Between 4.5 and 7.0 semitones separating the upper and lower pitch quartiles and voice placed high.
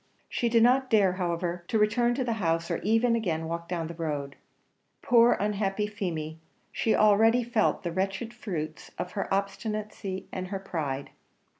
Yes: average, 4.8 semitones; high, 195 Hz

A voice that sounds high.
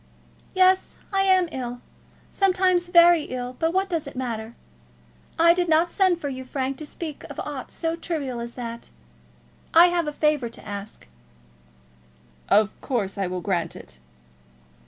Yes: very high, 295 Hz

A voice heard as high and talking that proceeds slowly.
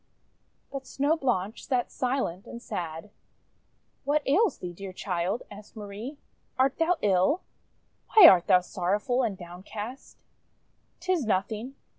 Yes: high, 215 Hz; slow, 125 wpm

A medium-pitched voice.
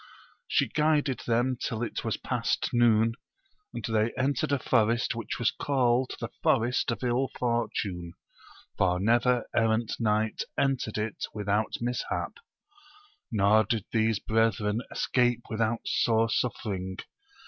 No: low, 115 Hz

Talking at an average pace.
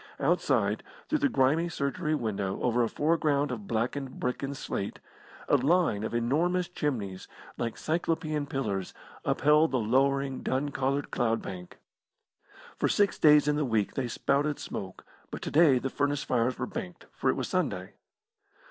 Yes: average, 160 wpm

